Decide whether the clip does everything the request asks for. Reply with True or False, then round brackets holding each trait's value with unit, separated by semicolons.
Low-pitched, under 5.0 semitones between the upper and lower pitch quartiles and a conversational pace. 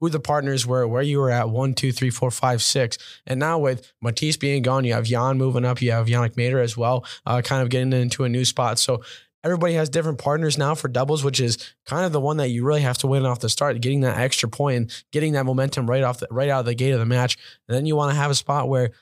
False (130 Hz; 2.4 semitones; 285 wpm)